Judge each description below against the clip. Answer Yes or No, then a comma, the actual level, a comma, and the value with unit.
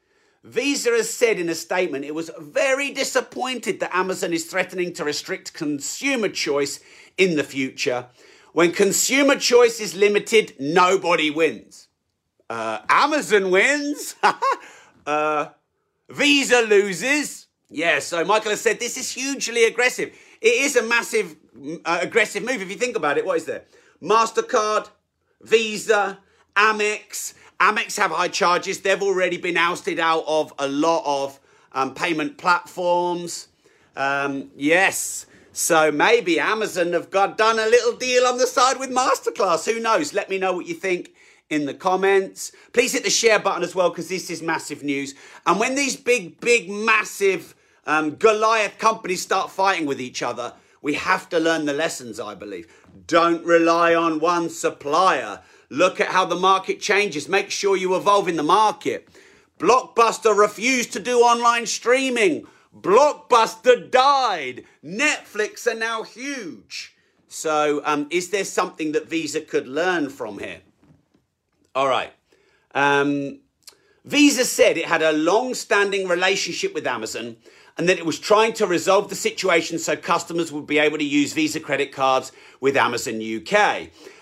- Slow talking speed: No, average, 155 wpm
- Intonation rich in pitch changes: Yes, wide, 6.1 semitones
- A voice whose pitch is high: Yes, high, 195 Hz